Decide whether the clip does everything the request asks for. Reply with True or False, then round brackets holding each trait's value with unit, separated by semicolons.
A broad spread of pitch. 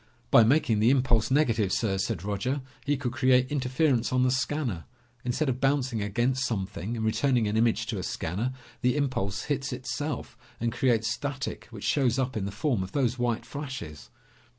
False (3.4 semitones)